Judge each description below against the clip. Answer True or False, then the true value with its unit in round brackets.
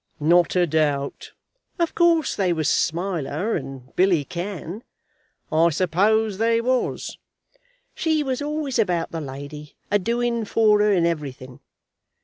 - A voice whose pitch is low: False (185 Hz)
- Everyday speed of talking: False (130 wpm)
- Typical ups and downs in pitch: False (6.6 semitones)